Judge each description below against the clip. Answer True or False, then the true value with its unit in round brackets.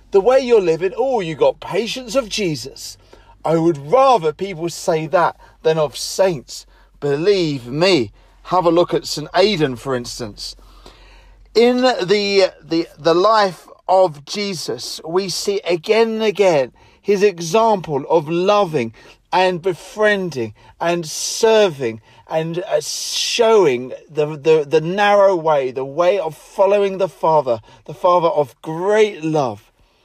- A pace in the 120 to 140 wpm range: True (135 wpm)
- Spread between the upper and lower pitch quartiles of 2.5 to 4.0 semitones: False (5.1 semitones)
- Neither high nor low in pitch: True (180 Hz)